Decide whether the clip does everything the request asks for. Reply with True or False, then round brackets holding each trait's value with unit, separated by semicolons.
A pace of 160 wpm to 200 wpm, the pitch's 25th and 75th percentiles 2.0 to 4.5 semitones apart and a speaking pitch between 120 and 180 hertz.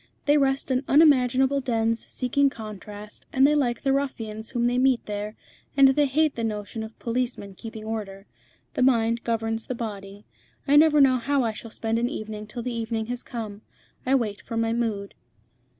False (185 wpm; 3.3 semitones; 235 Hz)